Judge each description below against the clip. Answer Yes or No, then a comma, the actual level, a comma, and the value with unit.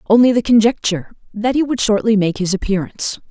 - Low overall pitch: No, high, 215 Hz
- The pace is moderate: Yes, average, 180 wpm